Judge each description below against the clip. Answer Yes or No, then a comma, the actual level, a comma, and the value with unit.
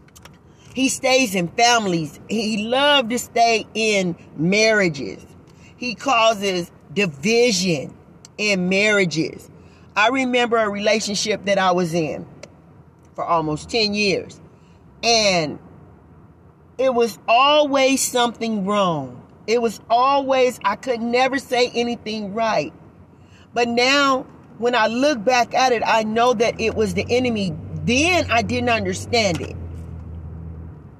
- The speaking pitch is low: No, high, 225 Hz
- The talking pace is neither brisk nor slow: No, slow, 120 wpm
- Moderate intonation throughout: Yes, average, 4.3 semitones